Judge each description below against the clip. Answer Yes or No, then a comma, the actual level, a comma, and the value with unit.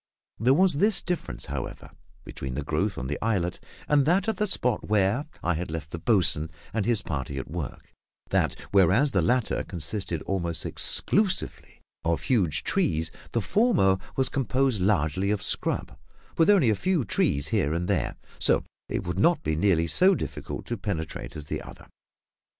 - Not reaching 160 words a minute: No, average, 175 wpm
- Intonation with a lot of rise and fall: Yes, wide, 8.5 semitones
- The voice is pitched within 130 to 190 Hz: No, very low, 95 Hz